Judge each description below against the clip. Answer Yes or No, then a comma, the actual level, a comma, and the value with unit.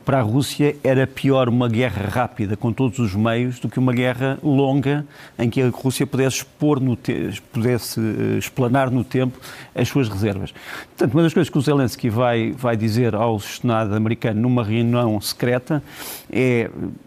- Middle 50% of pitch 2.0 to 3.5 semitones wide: Yes, average, 2.7 semitones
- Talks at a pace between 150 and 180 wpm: Yes, average, 170 wpm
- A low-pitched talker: Yes, low, 125 Hz